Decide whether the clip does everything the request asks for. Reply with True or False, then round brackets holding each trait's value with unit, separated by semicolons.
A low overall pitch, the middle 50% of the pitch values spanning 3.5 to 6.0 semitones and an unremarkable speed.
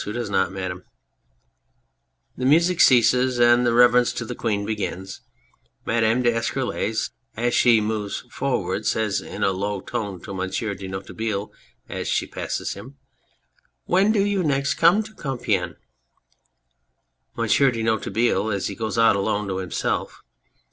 True (110 Hz; 3.9 semitones; 155 wpm)